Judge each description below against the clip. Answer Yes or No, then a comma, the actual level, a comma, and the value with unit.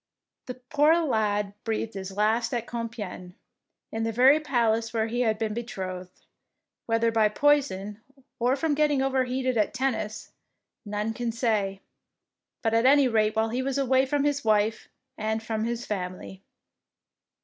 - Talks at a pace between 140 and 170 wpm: Yes, average, 155 wpm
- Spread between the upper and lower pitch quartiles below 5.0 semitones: Yes, average, 3.3 semitones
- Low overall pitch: No, high, 225 Hz